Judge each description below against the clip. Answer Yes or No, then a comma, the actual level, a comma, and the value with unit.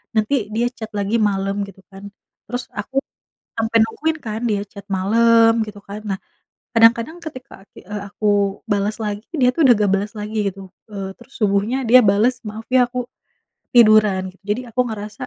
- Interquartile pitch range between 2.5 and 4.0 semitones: Yes, average, 2.8 semitones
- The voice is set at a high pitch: Yes, high, 215 Hz